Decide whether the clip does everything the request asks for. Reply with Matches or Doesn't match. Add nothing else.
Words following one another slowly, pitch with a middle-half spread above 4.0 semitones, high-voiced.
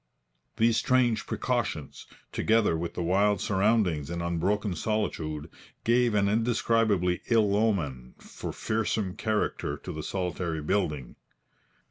Doesn't match